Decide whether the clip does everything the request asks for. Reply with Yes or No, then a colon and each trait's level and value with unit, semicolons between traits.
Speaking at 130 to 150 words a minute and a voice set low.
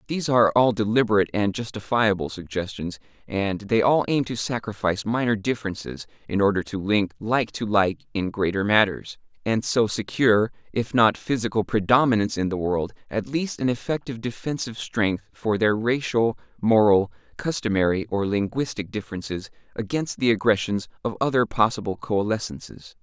Yes: average, 145 wpm; low, 110 Hz